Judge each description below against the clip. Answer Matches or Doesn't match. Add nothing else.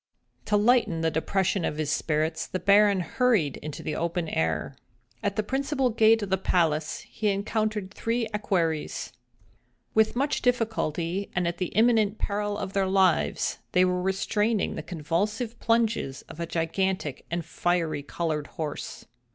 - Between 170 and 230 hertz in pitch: Matches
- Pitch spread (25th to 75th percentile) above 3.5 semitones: Matches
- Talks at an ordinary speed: Matches